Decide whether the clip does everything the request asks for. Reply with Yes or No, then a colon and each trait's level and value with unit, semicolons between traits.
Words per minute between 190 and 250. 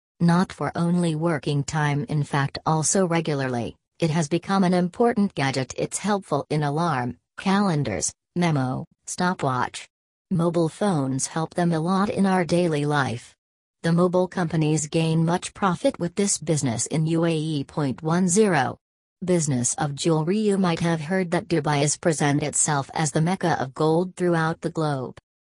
No: average, 150 wpm